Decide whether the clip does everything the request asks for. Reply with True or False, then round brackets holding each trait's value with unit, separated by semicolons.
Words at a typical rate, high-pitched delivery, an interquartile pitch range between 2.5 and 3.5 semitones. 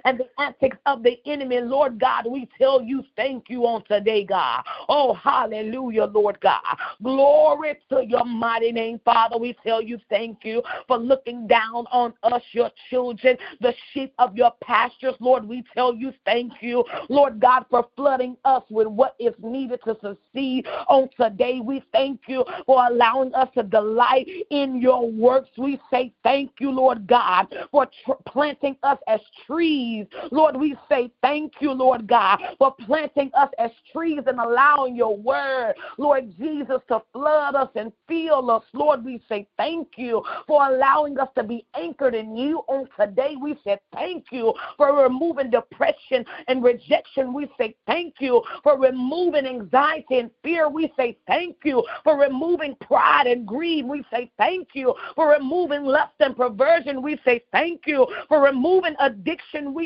True (170 wpm; 260 Hz; 3.1 semitones)